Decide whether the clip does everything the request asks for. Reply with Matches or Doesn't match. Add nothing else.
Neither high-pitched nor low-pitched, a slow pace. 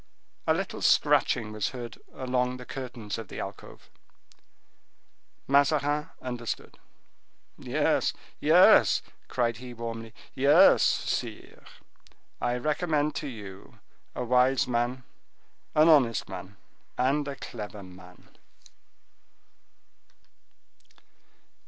Doesn't match